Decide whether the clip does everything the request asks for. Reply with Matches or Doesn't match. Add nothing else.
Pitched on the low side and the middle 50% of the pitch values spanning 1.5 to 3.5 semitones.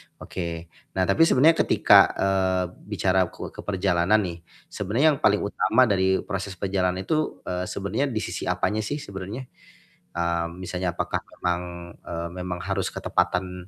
Matches